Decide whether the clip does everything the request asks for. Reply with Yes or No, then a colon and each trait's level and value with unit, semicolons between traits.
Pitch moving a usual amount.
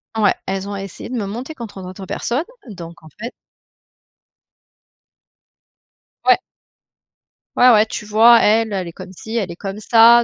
Yes: average, 3.3 semitones